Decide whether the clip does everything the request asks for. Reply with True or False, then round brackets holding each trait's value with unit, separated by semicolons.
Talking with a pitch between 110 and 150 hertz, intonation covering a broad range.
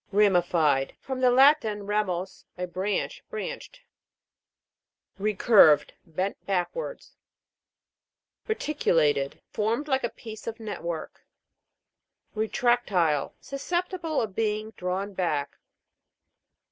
False (210 Hz; 5.9 semitones)